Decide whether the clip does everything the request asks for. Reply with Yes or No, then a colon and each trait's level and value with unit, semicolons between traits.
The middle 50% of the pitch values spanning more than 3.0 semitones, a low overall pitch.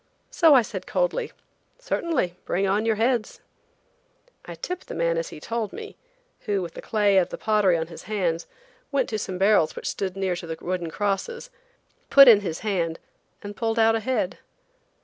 No: average, 4.5 semitones; high, 205 Hz